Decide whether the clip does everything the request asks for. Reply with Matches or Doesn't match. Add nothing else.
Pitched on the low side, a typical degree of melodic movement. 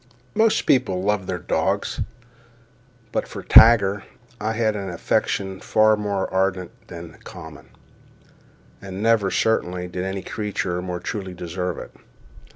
Matches